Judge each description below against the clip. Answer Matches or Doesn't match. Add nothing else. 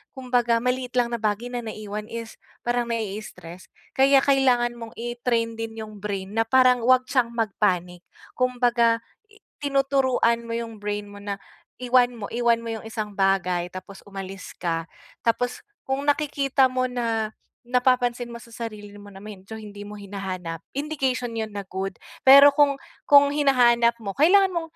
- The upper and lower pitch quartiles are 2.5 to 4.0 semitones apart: Matches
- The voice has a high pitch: Matches